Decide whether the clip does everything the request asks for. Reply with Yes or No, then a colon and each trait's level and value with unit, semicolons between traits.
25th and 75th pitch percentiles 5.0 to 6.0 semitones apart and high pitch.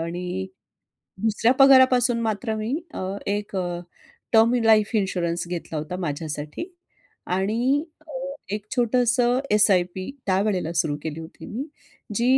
Yes: average, 5.3 semitones; high, 205 Hz